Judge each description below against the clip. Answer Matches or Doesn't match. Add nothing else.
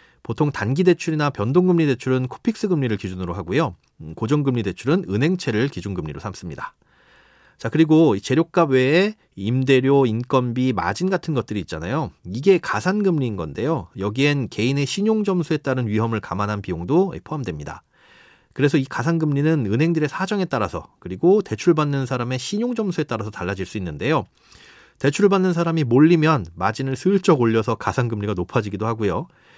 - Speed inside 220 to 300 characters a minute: Doesn't match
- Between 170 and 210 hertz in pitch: Doesn't match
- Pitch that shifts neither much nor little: Doesn't match